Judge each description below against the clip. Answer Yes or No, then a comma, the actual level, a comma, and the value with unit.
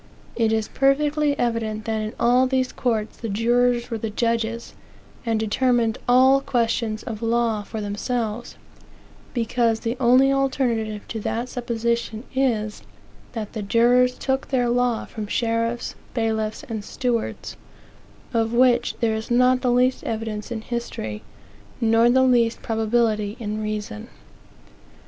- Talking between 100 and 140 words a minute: Yes, slow, 135 wpm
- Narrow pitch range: Yes, narrow, 2.0 semitones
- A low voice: No, high, 230 Hz